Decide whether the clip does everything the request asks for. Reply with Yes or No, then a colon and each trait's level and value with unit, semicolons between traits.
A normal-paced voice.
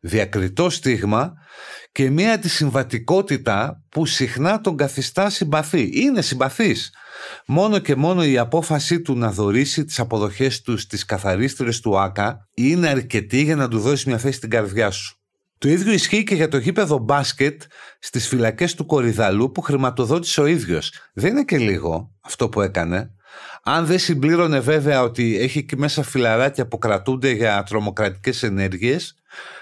Yes: average, 150 wpm